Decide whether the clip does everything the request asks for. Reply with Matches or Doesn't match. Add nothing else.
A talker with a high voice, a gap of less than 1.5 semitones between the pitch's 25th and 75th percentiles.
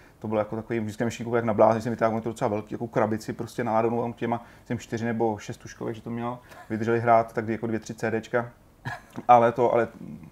Doesn't match